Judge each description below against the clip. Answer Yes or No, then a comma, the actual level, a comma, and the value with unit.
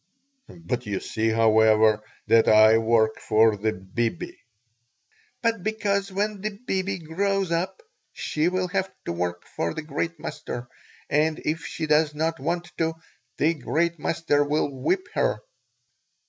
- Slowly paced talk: No, average, 145 wpm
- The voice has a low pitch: No, medium, 155 Hz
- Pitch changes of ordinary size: No, wide, 8.4 semitones